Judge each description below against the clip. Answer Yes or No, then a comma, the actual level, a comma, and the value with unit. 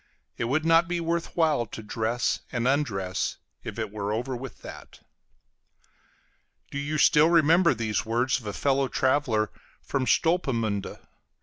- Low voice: Yes, low, 130 Hz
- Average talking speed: Yes, average, 145 wpm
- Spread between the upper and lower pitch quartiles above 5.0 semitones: Yes, wide, 5.6 semitones